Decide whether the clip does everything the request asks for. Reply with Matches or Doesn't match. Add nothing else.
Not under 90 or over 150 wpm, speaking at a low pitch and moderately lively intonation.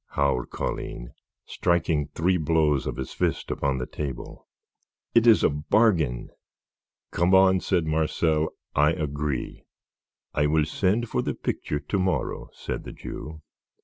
Matches